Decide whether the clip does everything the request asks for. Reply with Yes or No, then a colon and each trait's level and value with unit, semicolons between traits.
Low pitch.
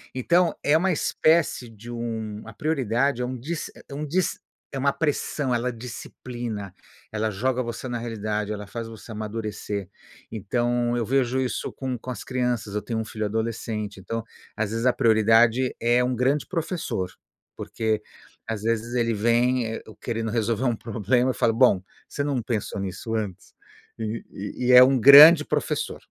Yes: low, 120 Hz